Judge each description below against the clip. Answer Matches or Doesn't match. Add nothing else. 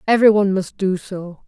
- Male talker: Doesn't match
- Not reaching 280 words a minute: Matches